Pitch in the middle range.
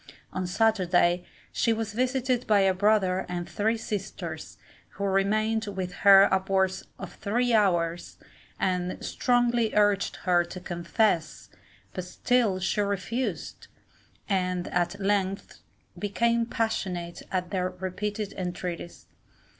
No: high, 195 Hz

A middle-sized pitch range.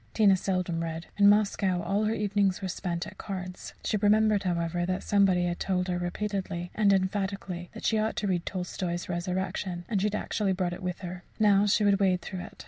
No: narrow, 2.3 semitones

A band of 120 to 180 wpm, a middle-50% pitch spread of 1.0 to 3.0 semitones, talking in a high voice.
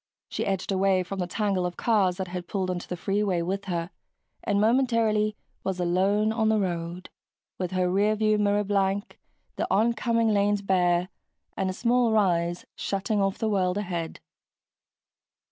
Yes: average, 160 wpm; average, 2.7 semitones; high, 195 Hz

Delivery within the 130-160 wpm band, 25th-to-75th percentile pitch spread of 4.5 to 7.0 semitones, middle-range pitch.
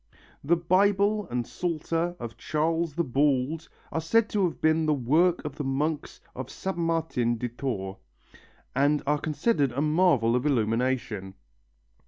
Yes: average, 150 wpm; average, 4.9 semitones; medium, 150 Hz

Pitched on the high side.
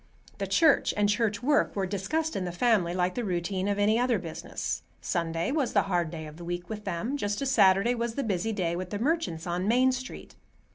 Yes: high, 205 Hz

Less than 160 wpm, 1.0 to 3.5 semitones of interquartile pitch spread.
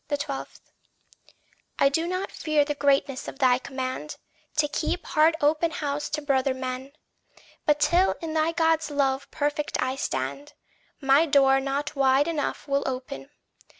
Yes: average, 150 wpm; narrow, 2.4 semitones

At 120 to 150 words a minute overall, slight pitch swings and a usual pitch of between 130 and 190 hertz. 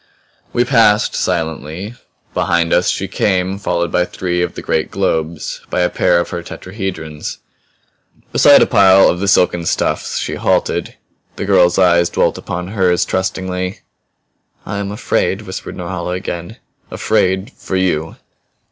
No: average, 145 wpm; narrow, 2.0 semitones; very low, 90 Hz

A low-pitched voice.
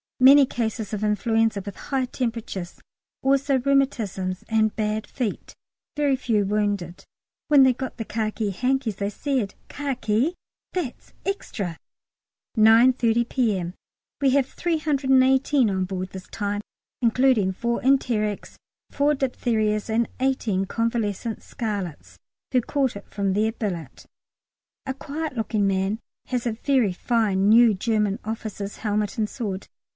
No: high, 225 Hz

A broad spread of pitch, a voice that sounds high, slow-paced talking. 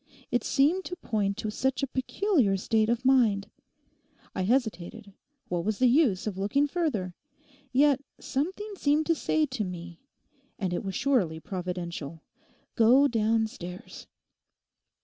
Yes: wide, 6.5 semitones; high, 225 Hz; slow, 130 wpm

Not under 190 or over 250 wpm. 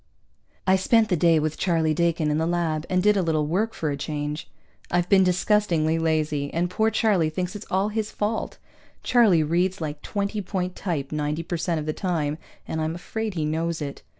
Yes: fast, 205 wpm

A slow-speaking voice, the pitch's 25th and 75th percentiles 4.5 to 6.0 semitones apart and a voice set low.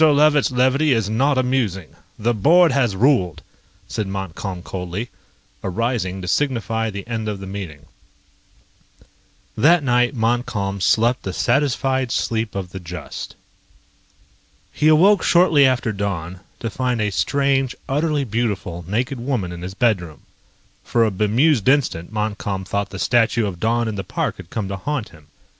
No: average, 150 wpm; average, 5.3 semitones; low, 115 Hz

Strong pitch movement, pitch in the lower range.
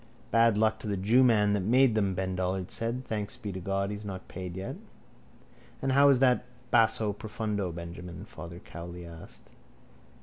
No: average, 3.5 semitones; low, 100 Hz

